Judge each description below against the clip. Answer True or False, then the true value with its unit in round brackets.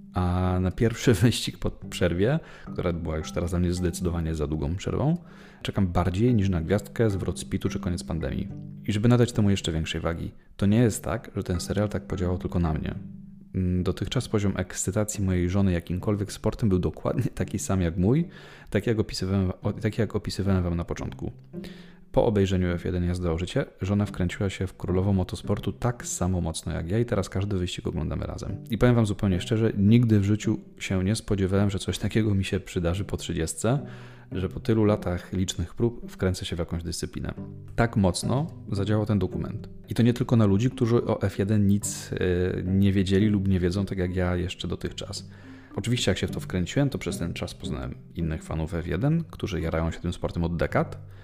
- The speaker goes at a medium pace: False (195 wpm)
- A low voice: True (95 Hz)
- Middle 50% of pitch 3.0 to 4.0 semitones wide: True (3.5 semitones)